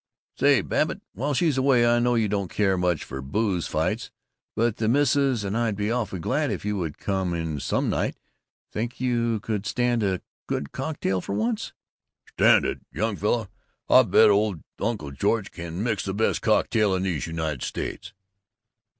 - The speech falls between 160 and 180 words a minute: Yes, average, 175 wpm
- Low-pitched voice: Yes, low, 105 Hz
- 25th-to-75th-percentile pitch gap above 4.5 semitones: No, average, 4.2 semitones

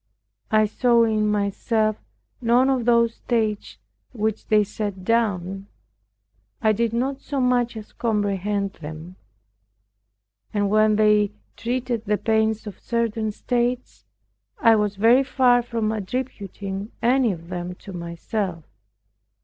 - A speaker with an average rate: No, slow, 125 wpm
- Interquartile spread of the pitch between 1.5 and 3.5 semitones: Yes, average, 2.7 semitones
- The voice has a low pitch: No, high, 215 Hz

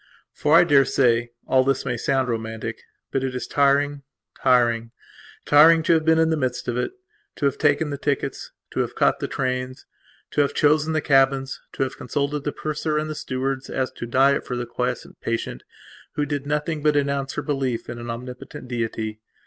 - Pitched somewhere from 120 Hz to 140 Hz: Yes, low, 135 Hz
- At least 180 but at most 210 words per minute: Yes, average, 195 wpm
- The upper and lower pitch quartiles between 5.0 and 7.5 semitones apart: No, average, 2.9 semitones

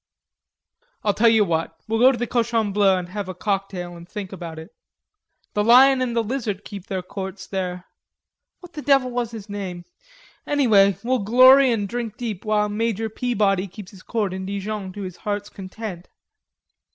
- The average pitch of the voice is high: Yes, high, 205 Hz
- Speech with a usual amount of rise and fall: Yes, average, 3.5 semitones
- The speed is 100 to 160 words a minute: No, average, 180 wpm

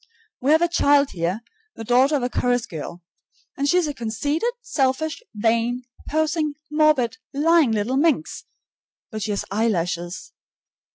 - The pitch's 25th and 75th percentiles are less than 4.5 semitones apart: No, wide, 5.6 semitones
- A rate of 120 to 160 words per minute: Yes, average, 150 wpm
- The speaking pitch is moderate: No, very high, 260 Hz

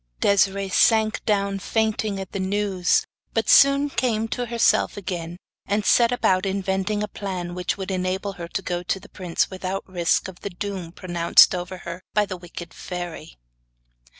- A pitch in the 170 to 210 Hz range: Yes, high, 190 Hz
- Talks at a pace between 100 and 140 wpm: No, average, 165 wpm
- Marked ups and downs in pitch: No, narrow, 2.5 semitones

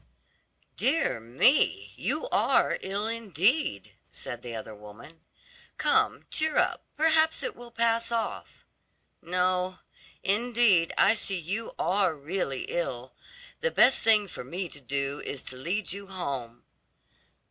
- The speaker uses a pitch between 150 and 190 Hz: Yes, medium, 185 Hz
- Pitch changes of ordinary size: No, wide, 8.6 semitones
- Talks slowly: Yes, slow, 130 wpm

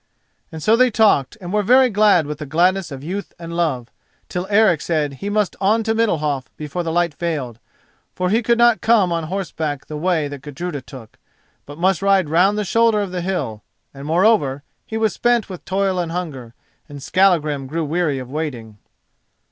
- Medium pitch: Yes, medium, 175 Hz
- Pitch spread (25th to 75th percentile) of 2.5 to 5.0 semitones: No, wide, 5.5 semitones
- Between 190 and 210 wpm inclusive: Yes, average, 195 wpm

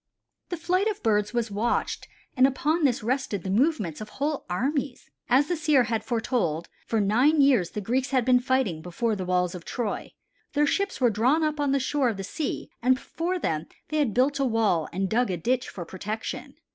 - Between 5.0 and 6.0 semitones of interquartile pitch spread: Yes, wide, 5.5 semitones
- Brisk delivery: Yes, fast, 210 wpm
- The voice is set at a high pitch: Yes, high, 245 Hz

